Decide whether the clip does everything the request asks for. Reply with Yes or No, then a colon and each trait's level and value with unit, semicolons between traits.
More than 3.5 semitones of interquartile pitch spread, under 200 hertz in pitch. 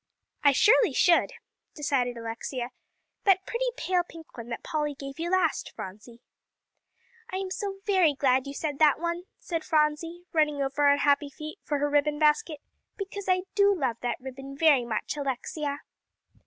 No: average, 4.2 semitones; very high, 300 Hz